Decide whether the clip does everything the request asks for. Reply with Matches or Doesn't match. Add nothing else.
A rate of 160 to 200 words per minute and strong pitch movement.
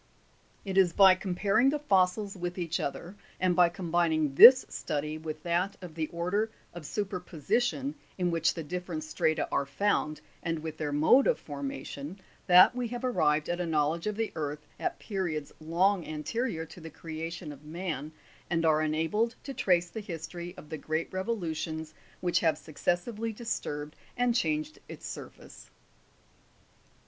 Doesn't match